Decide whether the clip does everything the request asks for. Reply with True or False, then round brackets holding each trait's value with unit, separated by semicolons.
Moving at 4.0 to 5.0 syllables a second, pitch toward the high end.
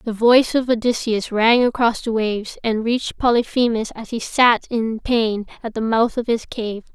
True (4.8 syllables/s; 230 Hz)